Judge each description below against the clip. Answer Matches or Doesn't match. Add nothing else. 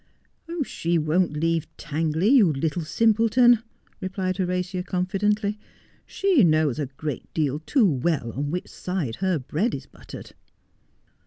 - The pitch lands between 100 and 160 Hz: Doesn't match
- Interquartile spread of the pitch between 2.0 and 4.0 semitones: Doesn't match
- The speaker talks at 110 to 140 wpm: Matches